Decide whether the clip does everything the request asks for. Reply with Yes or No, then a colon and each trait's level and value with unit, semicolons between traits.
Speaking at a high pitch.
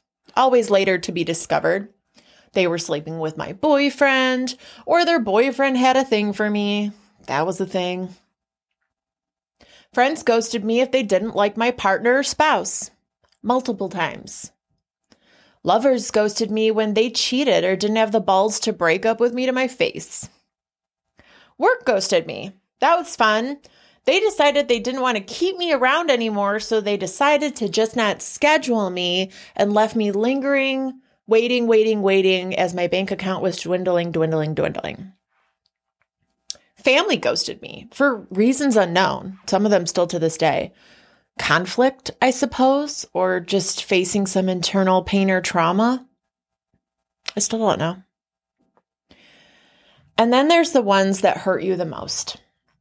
Yes: high, 210 Hz